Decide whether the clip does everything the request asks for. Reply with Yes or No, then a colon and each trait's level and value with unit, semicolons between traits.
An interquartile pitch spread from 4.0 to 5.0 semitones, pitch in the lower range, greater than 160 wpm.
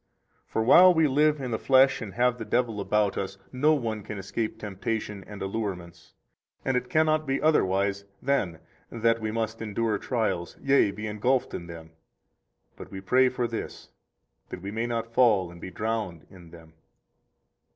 Yes: average, 4.5 semitones; low, 110 Hz; average, 170 wpm